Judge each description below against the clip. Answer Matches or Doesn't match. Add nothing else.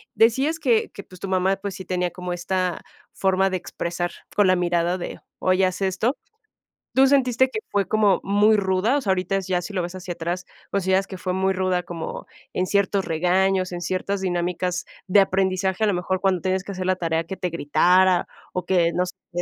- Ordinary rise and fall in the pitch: Doesn't match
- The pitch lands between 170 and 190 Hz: Matches